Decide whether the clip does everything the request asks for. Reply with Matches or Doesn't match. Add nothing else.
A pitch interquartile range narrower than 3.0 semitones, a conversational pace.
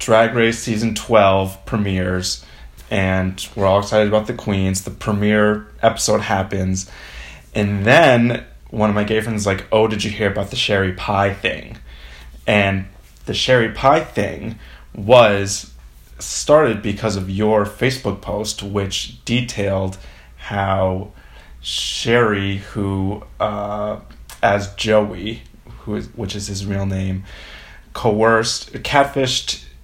Doesn't match